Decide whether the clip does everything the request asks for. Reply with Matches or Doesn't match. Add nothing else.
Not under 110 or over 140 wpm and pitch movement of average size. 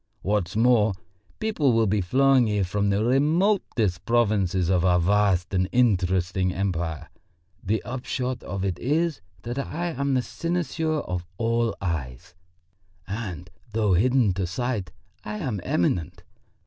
Doesn't match